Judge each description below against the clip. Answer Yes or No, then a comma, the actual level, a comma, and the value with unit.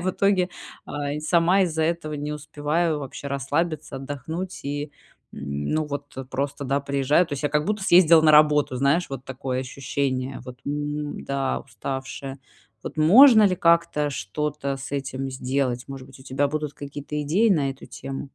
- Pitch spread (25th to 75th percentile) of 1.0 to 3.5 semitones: Yes, narrow, 2.5 semitones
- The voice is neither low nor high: Yes, medium, 145 Hz